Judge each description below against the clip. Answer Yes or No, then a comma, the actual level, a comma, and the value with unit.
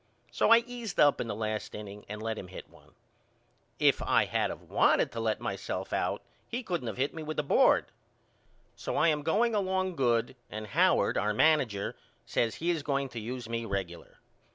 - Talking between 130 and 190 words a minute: No, average, 200 wpm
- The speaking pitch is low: Yes, low, 130 Hz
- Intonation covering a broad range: Yes, wide, 7.3 semitones